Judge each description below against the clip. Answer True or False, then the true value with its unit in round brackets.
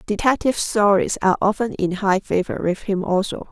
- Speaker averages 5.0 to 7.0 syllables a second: True (5.5 syllables/s)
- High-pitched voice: True (200 Hz)